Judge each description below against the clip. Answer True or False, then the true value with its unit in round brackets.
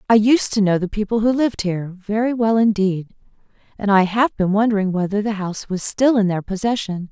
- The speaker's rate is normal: True (195 wpm)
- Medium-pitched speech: False (205 Hz)